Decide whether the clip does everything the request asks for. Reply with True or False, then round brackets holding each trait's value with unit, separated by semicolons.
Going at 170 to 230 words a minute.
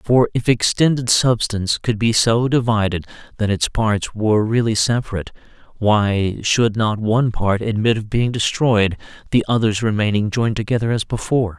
False (155 wpm)